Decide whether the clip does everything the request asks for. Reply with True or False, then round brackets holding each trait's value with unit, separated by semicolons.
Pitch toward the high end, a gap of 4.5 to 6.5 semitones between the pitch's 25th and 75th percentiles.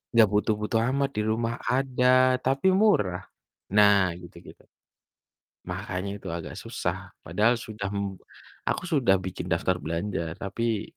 False (105 Hz; 5.1 semitones)